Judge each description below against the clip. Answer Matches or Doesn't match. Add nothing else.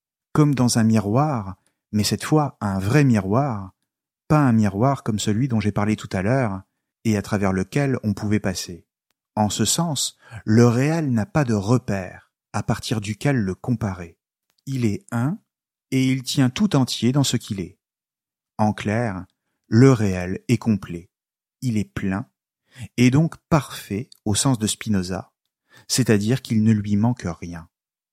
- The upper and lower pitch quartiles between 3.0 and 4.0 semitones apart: Doesn't match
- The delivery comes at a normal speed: Matches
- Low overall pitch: Matches